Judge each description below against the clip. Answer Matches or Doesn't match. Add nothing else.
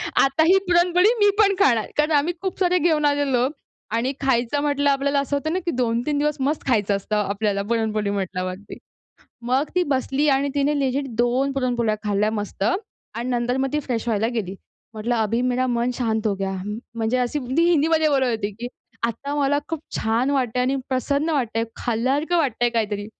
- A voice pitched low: Doesn't match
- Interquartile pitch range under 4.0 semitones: Doesn't match